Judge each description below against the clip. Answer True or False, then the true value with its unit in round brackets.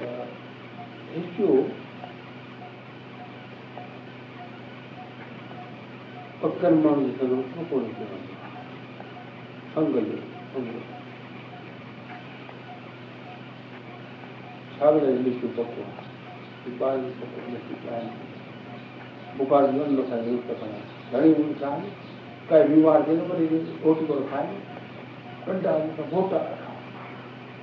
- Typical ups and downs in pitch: True (4.2 semitones)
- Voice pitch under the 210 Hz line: True (140 Hz)